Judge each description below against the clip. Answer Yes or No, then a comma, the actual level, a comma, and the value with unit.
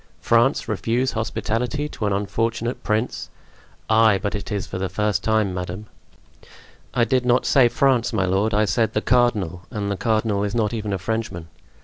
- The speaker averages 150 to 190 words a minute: Yes, average, 175 wpm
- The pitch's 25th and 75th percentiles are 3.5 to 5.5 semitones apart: No, average, 2.7 semitones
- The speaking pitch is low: Yes, low, 110 Hz